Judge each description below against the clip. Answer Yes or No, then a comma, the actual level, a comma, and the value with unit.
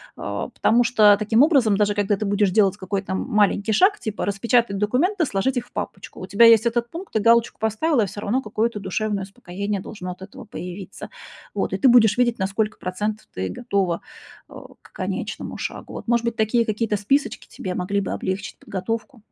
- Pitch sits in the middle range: No, high, 215 Hz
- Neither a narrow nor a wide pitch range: Yes, average, 3.0 semitones